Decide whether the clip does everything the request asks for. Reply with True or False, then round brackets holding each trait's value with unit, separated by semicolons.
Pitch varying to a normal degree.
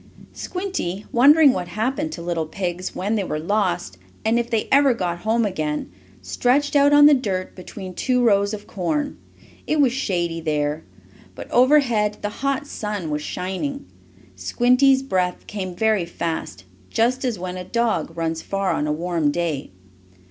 False (6.6 semitones)